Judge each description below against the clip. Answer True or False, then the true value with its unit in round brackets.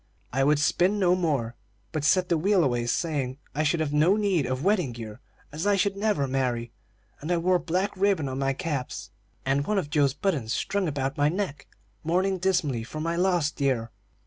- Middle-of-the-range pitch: True (155 Hz)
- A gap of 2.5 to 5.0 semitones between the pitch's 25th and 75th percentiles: False (5.4 semitones)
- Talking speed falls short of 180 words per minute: False (200 wpm)